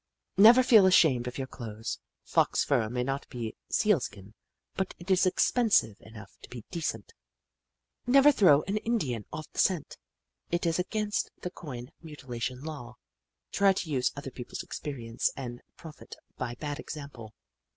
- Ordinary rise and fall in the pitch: No, wide, 7.5 semitones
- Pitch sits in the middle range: Yes, medium, 145 Hz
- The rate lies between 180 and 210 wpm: No, average, 160 wpm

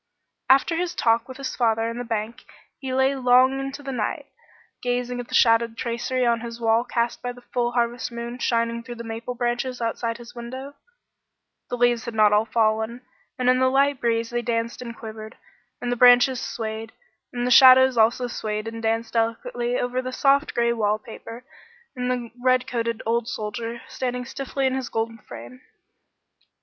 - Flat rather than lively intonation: Yes, narrow, 1.8 semitones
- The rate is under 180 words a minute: No, average, 185 wpm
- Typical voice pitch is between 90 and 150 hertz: No, high, 240 Hz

